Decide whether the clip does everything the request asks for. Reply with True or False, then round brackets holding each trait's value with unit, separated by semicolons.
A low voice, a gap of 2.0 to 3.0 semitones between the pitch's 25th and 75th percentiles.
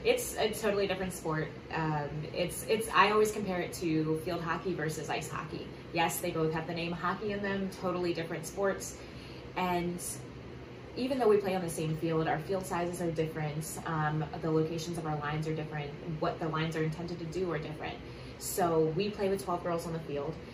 False (170 Hz; 2.5 semitones)